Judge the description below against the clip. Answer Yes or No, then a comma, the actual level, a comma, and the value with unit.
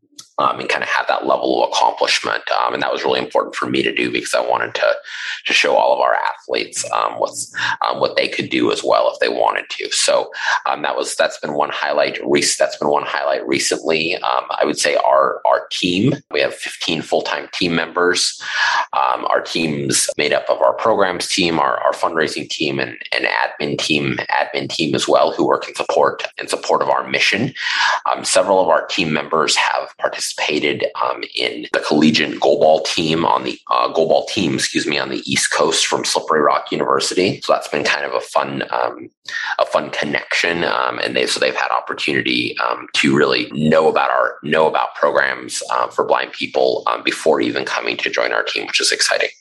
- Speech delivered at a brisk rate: Yes, fast, 210 wpm